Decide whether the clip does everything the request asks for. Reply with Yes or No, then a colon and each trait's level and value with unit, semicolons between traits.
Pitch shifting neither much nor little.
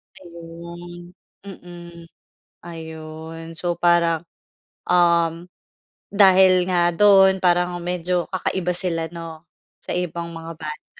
No: narrow, 1.2 semitones